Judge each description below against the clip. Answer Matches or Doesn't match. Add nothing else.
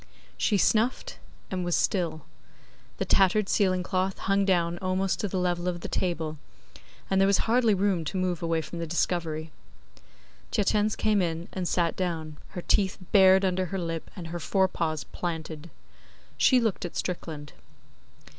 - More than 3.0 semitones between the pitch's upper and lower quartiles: Doesn't match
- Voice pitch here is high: Doesn't match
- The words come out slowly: Doesn't match